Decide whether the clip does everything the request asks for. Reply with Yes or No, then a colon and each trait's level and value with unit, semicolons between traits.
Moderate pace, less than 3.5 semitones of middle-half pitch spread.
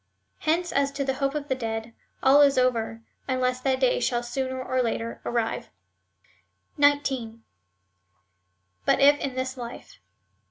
Yes: average, 145 wpm; narrow, 2.6 semitones